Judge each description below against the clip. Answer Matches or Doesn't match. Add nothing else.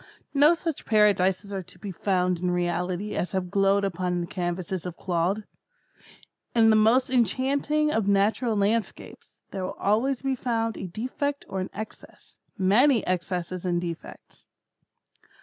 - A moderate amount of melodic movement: Matches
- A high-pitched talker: Matches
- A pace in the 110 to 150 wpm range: Matches